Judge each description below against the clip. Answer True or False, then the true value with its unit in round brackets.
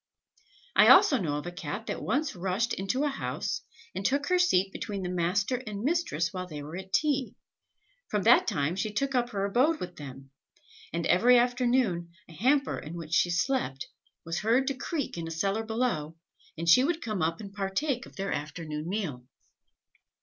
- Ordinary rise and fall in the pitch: False (6.7 semitones)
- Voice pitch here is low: False (195 Hz)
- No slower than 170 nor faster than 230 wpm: True (190 wpm)